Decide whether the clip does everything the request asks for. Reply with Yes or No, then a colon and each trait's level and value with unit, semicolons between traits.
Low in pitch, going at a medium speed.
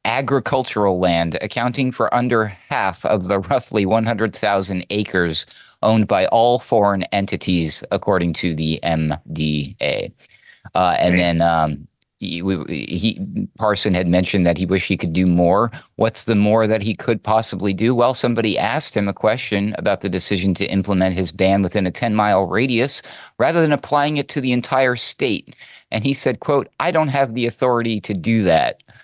Yes: low, 105 Hz; average, 175 wpm